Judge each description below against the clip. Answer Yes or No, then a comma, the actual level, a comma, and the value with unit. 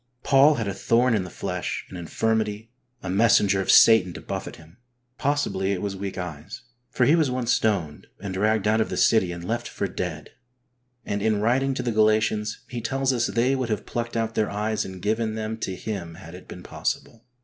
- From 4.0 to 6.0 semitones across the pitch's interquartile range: No, average, 3.6 semitones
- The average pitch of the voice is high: No, low, 110 Hz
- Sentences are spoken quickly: Yes, fast, 210 wpm